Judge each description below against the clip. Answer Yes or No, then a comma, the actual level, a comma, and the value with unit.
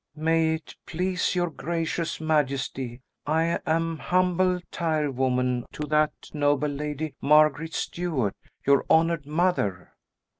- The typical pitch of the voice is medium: Yes, medium, 155 Hz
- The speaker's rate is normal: No, slow, 110 wpm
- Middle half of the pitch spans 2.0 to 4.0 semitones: Yes, average, 2.9 semitones